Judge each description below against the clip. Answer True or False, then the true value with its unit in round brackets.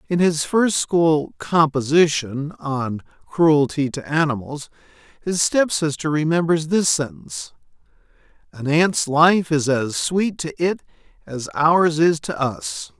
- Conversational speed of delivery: False (125 wpm)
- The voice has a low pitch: False (155 Hz)